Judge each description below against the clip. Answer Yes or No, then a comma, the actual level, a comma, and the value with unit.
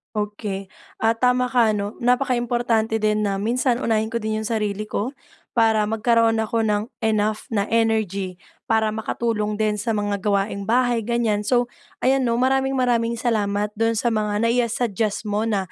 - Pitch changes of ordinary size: No, narrow, 2.1 semitones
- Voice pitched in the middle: No, high, 220 Hz